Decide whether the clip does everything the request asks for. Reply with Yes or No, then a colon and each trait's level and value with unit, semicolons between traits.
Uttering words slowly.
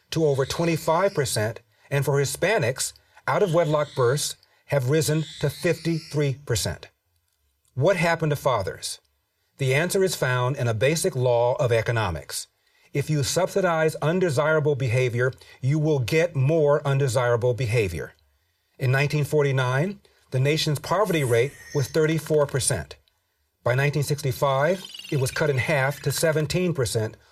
Yes: slow, 125 wpm